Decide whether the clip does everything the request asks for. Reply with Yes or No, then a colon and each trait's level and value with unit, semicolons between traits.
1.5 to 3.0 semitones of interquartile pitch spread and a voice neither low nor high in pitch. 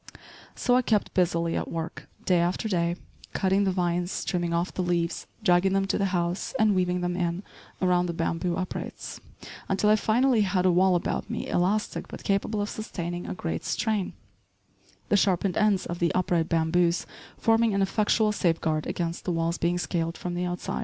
Yes: narrow, 2.5 semitones; medium, 180 Hz